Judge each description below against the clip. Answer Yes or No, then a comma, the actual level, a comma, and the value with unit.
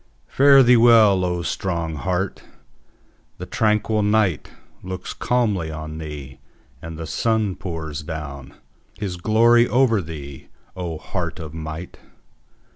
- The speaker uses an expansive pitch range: Yes, wide, 5.7 semitones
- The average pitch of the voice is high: No, very low, 90 Hz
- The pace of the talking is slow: Yes, slow, 115 wpm